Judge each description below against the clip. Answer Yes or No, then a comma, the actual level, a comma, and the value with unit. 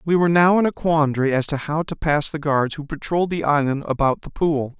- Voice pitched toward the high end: No, medium, 150 Hz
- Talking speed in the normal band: No, fast, 250 wpm